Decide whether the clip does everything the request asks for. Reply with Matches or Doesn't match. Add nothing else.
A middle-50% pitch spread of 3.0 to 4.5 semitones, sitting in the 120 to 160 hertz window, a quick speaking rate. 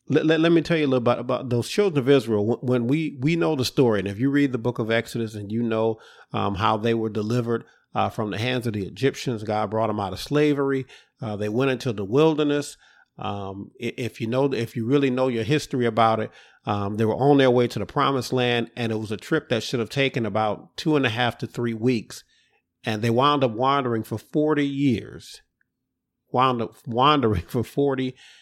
Matches